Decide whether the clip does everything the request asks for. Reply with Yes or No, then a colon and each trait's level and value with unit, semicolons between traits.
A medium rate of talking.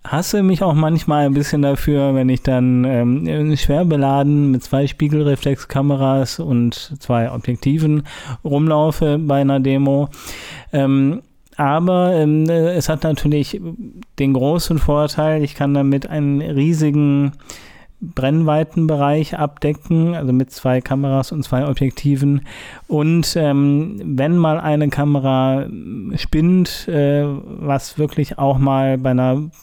No: slow, 120 wpm